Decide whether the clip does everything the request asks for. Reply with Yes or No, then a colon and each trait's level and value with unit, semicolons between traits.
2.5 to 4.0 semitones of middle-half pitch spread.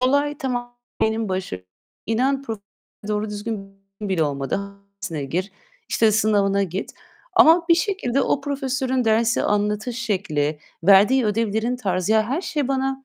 No: average, 4.8 semitones